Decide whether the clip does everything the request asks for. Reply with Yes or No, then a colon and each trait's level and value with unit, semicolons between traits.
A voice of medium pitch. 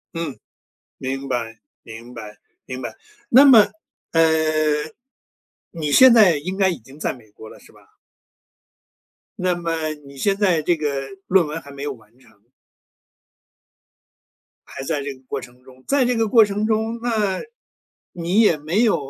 Yes: medium, 160 Hz